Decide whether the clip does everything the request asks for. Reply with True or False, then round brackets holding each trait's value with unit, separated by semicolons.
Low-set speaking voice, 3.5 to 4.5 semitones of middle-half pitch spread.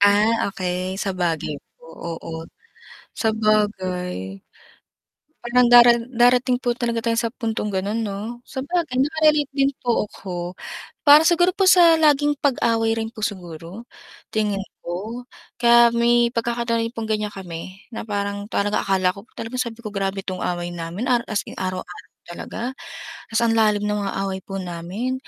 False (220 Hz; 4.1 semitones)